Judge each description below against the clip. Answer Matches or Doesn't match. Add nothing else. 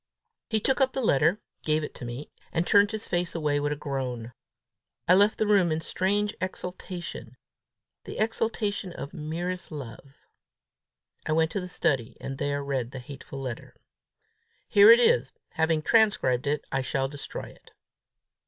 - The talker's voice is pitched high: Doesn't match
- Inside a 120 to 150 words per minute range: Doesn't match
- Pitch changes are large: Matches